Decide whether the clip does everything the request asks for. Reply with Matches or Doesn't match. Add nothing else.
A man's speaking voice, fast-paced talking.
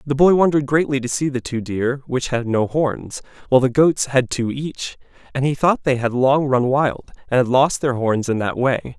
Matches